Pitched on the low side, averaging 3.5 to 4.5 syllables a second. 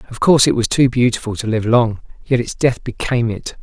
No: low, 120 Hz; 5.9 syllables/s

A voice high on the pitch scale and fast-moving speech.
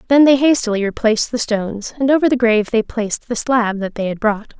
Yes: high, 230 Hz; fast, 235 wpm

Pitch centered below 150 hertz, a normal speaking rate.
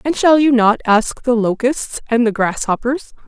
No: high, 240 Hz; average, 185 wpm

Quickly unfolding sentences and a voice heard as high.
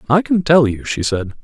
No: fast, 250 wpm; medium, 140 Hz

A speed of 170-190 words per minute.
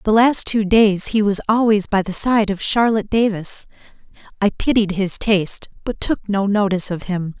Yes: average, 185 wpm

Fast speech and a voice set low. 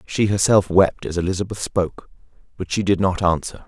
No: average, 180 wpm; very low, 95 Hz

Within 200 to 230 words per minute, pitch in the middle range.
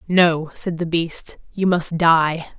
No: average, 160 wpm; medium, 170 Hz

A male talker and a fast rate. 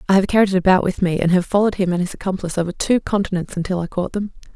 No: female; fast, 275 wpm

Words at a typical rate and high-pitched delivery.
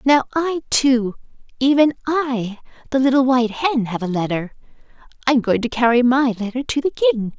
Yes: average, 180 wpm; very high, 255 Hz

